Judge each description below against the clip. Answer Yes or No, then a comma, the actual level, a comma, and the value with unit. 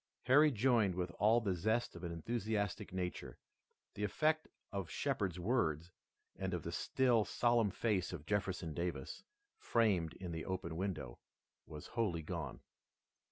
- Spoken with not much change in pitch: No, average, 5.2 semitones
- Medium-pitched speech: No, very low, 95 Hz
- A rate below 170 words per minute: Yes, average, 145 wpm